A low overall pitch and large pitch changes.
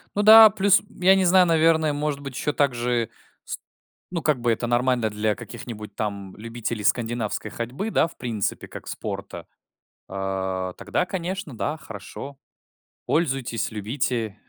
Yes: low, 125 Hz; wide, 6.7 semitones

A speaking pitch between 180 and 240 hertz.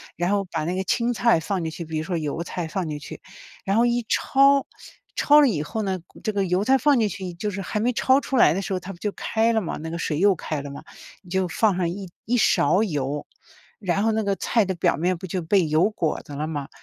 Yes: high, 190 Hz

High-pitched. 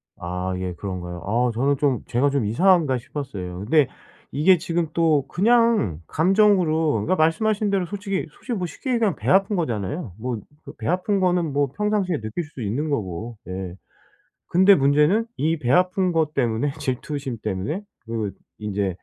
No: medium, 145 Hz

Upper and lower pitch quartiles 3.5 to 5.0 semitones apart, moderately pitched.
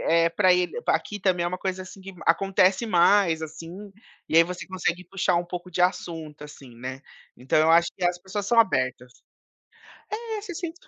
No: average, 2.8 semitones; medium, 180 Hz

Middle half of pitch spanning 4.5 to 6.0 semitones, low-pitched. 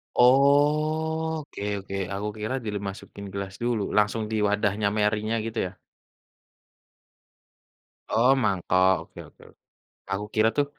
Yes: average, 5.2 semitones; low, 110 Hz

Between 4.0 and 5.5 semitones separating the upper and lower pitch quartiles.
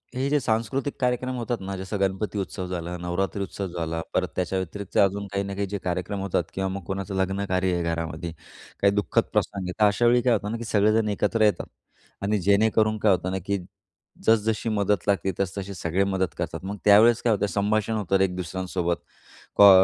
No: narrow, 2.4 semitones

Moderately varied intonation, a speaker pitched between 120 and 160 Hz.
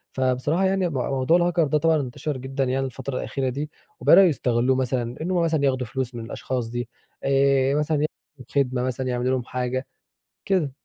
Yes: average, 3.0 semitones; low, 135 Hz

